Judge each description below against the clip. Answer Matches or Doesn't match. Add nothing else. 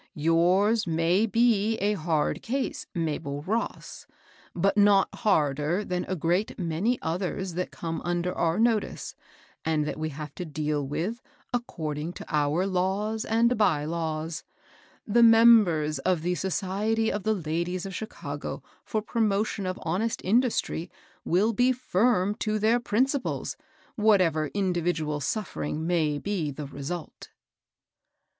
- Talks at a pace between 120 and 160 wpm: Matches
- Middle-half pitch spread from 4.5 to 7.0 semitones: Matches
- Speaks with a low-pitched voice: Doesn't match